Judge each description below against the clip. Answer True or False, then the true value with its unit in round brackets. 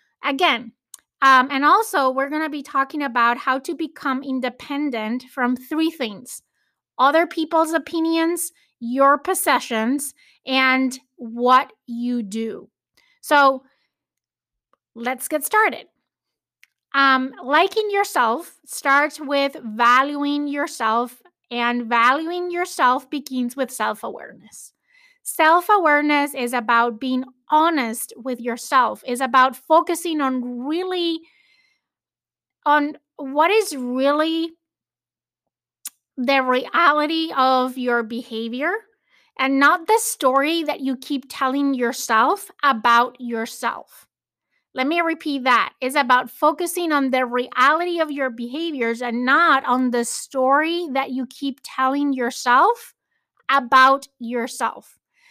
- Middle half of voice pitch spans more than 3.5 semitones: True (4.2 semitones)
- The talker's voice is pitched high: True (275 Hz)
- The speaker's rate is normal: False (110 wpm)